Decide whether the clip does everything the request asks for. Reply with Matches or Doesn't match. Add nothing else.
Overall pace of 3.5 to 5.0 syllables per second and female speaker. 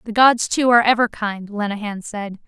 Doesn't match